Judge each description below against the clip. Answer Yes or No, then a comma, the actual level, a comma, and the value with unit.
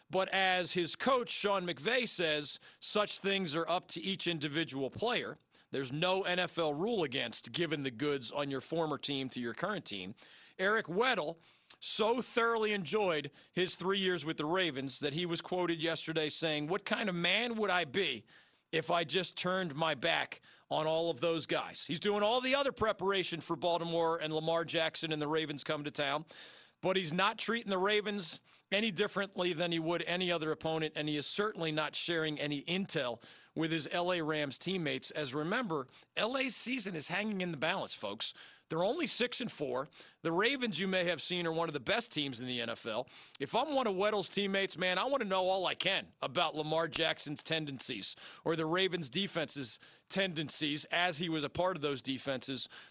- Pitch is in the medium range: Yes, medium, 170 Hz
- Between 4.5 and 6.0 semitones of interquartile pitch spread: No, average, 3.8 semitones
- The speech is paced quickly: No, average, 195 wpm